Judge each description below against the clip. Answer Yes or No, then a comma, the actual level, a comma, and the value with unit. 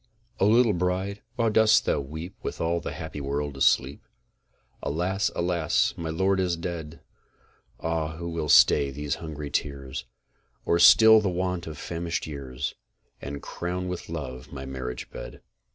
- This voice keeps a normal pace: Yes, average, 150 wpm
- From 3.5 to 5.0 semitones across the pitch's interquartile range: Yes, average, 4.1 semitones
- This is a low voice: Yes, very low, 80 Hz